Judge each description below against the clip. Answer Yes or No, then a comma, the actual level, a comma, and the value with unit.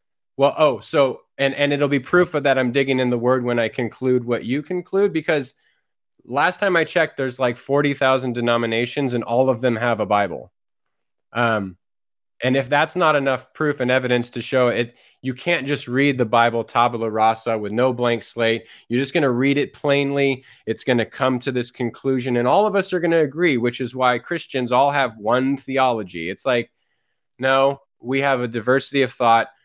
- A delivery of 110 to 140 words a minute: No, average, 200 wpm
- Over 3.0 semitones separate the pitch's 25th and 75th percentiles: No, average, 2.7 semitones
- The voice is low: Yes, low, 130 Hz